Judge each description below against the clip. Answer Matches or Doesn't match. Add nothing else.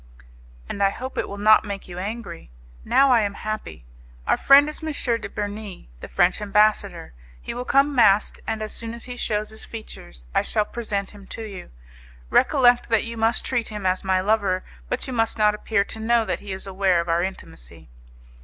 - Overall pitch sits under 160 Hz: Doesn't match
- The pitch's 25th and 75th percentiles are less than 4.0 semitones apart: Matches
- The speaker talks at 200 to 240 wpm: Matches